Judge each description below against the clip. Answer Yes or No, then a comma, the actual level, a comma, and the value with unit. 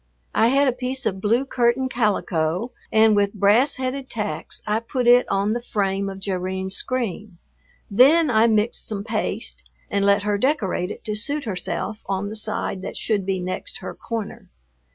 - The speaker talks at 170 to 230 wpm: Yes, average, 175 wpm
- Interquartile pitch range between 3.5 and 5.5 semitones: Yes, average, 3.8 semitones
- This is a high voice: Yes, high, 215 Hz